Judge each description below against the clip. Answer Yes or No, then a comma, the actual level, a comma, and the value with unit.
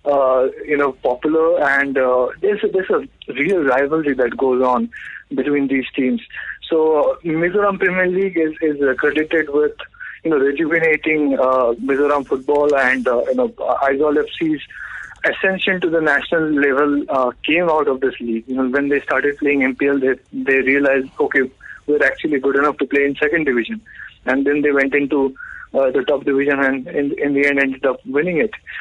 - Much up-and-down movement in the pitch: No, average, 2.8 semitones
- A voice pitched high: No, medium, 140 Hz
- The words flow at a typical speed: Yes, average, 185 wpm